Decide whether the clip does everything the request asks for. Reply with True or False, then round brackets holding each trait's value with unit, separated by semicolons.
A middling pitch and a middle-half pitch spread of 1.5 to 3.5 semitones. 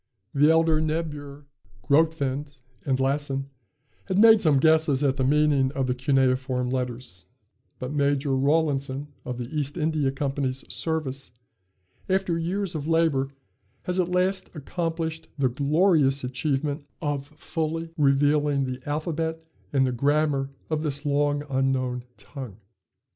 True (145 Hz; 3.0 semitones)